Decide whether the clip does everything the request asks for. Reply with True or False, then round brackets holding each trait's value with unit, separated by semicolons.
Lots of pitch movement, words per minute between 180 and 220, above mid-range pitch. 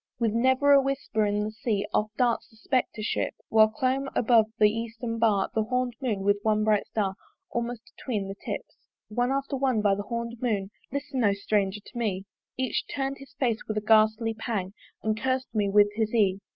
False (3.1 semitones; 200 wpm; 220 Hz)